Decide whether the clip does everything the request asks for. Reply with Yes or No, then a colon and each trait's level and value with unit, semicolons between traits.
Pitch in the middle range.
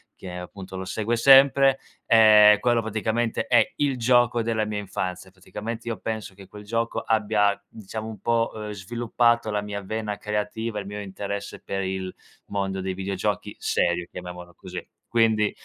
No: low, 105 Hz